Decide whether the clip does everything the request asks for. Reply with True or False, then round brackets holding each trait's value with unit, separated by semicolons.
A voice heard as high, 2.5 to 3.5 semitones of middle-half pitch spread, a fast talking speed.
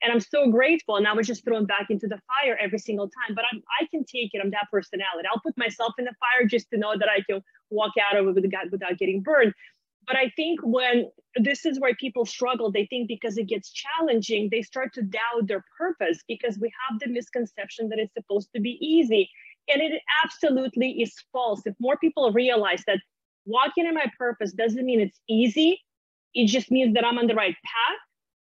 True (235 Hz; 3.2 semitones; 215 wpm)